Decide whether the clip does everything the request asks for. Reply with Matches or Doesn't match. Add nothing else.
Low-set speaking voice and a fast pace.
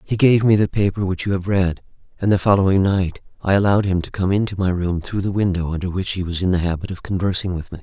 Matches